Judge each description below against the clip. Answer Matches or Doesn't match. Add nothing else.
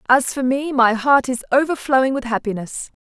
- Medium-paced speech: Matches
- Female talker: Matches